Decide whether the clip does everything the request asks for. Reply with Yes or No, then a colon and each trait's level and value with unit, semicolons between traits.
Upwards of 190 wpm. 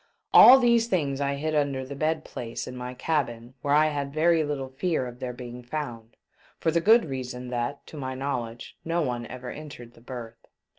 Yes: average, 200 wpm